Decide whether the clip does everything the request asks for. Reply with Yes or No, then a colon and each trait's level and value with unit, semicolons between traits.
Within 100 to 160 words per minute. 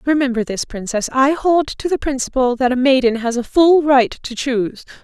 No: fast, 205 wpm